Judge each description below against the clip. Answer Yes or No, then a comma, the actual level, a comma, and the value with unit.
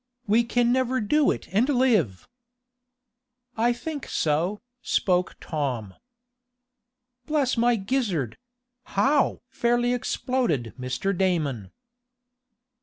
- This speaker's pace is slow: Yes, slow, 95 wpm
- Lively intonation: Yes, wide, 8.0 semitones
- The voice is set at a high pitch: Yes, high, 225 Hz